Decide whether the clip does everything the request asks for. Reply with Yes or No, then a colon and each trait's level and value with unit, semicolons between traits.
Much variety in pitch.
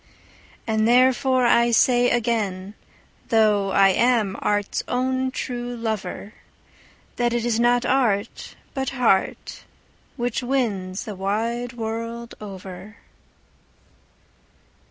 No: average, 3.0 semitones